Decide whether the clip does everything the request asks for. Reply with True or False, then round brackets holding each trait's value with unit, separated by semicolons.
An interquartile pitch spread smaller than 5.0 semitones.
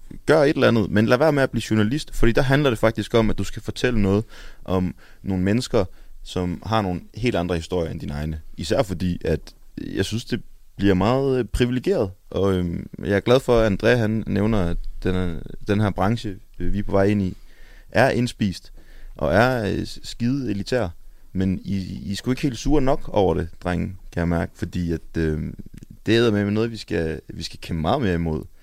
True (4.3 semitones)